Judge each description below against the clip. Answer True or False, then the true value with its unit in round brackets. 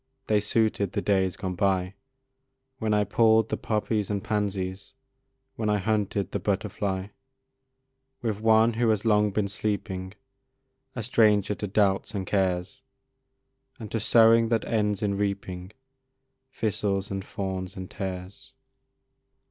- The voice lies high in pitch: False (105 Hz)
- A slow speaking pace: True (130 wpm)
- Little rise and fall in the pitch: True (2.2 semitones)